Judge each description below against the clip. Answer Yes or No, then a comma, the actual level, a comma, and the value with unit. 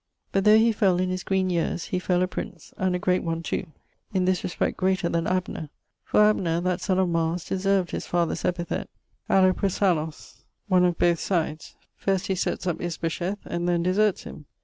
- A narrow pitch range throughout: Yes, narrow, 1.8 semitones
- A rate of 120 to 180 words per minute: No, average, 195 wpm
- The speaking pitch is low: No, medium, 180 Hz